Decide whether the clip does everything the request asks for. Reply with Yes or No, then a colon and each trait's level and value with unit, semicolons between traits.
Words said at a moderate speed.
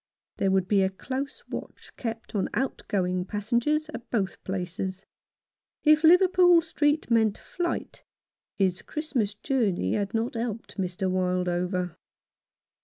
No: slow, 130 wpm